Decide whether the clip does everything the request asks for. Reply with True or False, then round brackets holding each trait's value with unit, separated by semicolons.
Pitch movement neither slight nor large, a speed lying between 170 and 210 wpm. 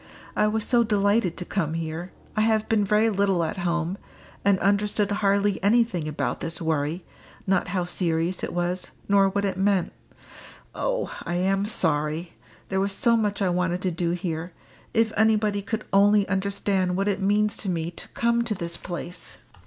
True (3.0 semitones; 175 wpm)